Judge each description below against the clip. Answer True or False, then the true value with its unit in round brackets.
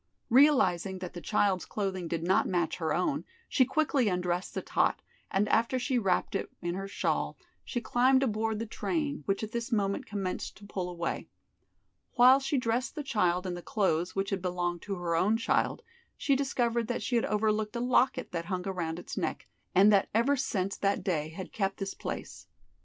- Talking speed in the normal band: True (195 wpm)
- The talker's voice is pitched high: True (200 Hz)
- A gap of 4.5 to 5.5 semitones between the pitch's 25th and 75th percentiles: True (5.0 semitones)